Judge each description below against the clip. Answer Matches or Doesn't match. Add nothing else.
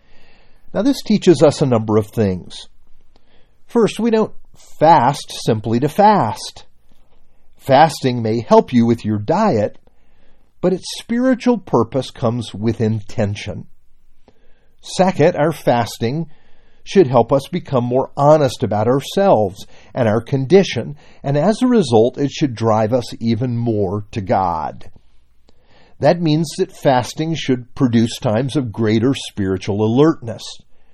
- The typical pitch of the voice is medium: Doesn't match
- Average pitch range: Doesn't match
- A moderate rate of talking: Doesn't match